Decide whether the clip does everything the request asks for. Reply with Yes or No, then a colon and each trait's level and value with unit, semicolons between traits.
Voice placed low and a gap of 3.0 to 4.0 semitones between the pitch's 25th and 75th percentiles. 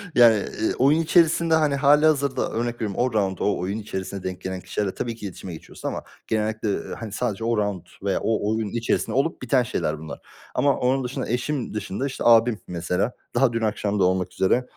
No: low, 110 Hz; average, 4.6 semitones